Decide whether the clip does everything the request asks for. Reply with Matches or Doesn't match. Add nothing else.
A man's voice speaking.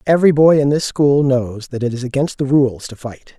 Matches